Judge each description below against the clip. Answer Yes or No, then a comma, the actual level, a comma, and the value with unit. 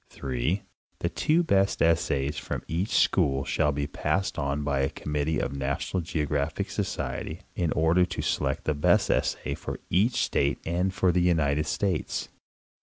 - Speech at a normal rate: Yes, average, 165 wpm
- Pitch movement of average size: Yes, average, 4.1 semitones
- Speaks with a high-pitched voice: No, very low, 80 Hz